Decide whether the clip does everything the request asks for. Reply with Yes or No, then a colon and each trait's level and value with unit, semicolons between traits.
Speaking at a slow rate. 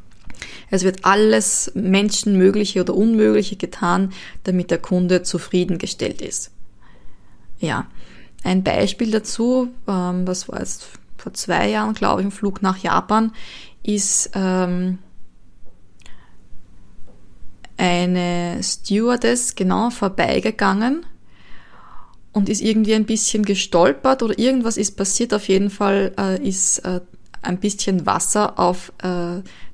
Yes: slow, 115 wpm